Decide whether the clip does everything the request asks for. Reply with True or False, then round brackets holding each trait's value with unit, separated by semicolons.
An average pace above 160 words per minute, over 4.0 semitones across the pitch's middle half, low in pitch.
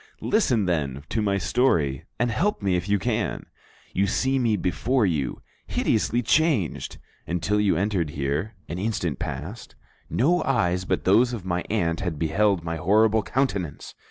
False (155 wpm; 5.0 semitones; 100 Hz)